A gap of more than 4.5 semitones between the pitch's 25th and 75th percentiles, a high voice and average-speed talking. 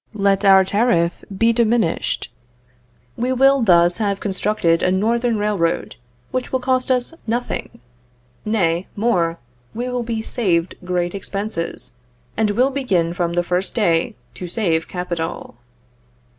No: average, 5.1 semitones; high, 200 Hz; slow, 130 wpm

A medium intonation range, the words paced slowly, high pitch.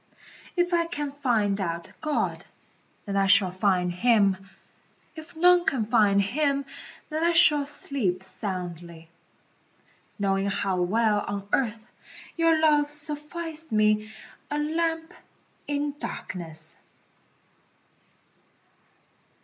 No: wide, 7.5 semitones; slow, 105 wpm; high, 225 Hz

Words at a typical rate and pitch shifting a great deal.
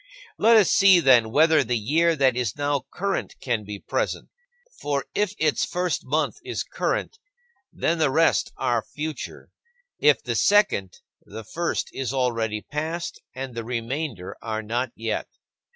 Yes: average, 150 wpm; wide, 6.0 semitones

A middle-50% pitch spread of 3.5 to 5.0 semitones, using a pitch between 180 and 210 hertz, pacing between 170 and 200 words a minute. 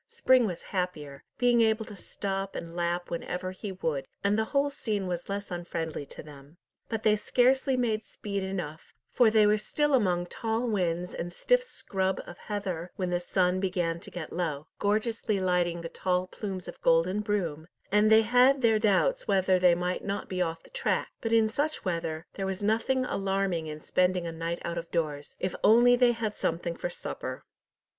Yes: average, 4.1 semitones; high, 190 Hz; average, 190 wpm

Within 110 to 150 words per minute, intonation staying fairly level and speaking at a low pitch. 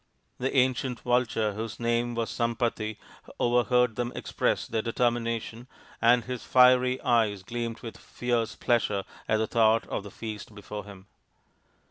Yes: average, 140 wpm; narrow, 1.9 semitones; low, 115 Hz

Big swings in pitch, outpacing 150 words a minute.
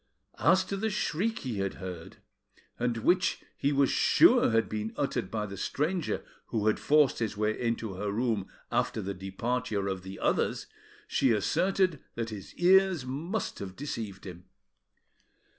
Yes: wide, 6.8 semitones; average, 160 wpm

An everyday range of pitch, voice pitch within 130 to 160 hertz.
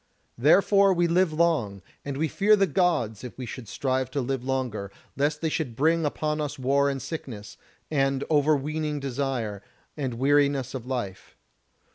Yes: average, 3.5 semitones; medium, 140 Hz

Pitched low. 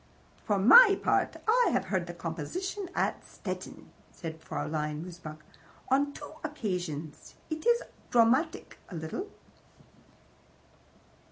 No: high, 195 Hz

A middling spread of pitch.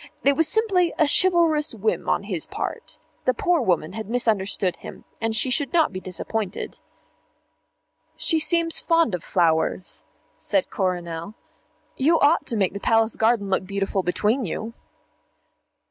No: wide, 8.0 semitones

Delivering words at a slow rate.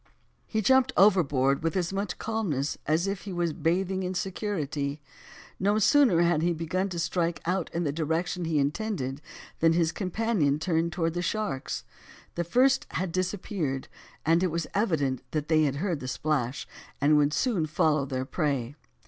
No: average, 165 wpm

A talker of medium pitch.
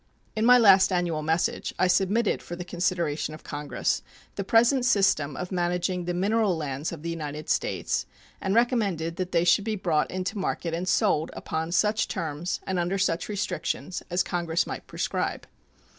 Yes: medium, 180 Hz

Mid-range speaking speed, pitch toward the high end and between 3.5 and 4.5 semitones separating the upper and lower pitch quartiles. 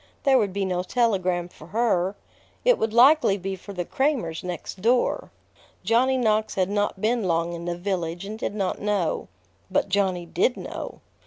Yes: average, 175 wpm; high, 195 Hz; average, 4.2 semitones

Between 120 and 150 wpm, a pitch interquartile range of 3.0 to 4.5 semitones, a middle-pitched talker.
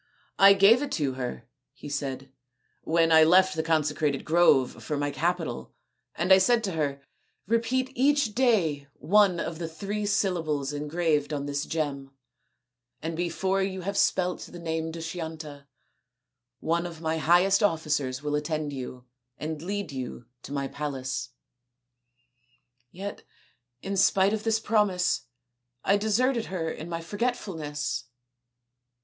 No: average, 145 wpm; average, 4.9 semitones; medium, 165 Hz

